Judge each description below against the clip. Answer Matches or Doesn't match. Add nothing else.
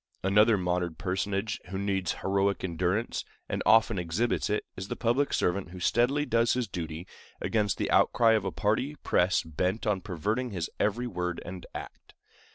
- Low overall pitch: Matches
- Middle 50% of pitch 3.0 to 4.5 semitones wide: Matches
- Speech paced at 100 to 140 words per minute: Doesn't match